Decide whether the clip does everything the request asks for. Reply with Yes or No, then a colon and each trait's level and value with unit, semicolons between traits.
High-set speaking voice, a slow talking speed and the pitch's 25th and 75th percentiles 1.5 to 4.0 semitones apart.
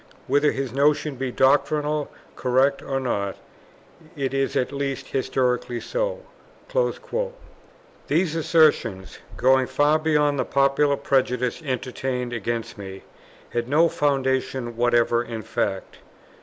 No: low, 135 Hz; slow, 115 wpm; average, 2.9 semitones